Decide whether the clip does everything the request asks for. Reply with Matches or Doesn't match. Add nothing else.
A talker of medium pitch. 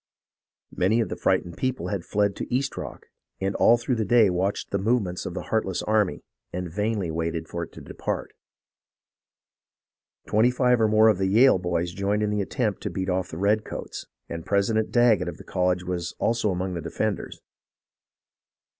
Doesn't match